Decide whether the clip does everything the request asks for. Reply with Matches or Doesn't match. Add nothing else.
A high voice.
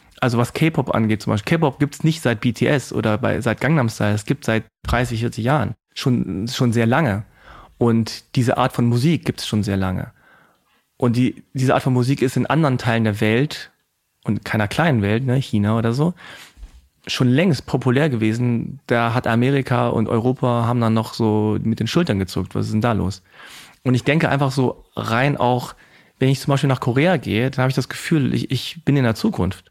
Doesn't match